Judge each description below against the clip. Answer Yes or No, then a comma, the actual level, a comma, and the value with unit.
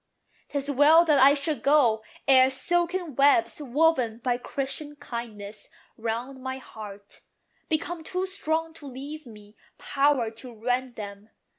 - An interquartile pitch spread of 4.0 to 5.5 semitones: Yes, average, 4.5 semitones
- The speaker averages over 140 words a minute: No, slow, 135 wpm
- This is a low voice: No, very high, 270 Hz